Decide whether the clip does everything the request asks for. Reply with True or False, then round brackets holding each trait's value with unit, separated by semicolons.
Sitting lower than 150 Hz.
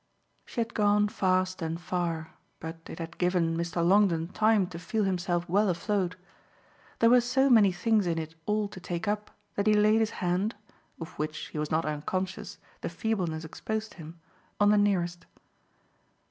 False (185 Hz)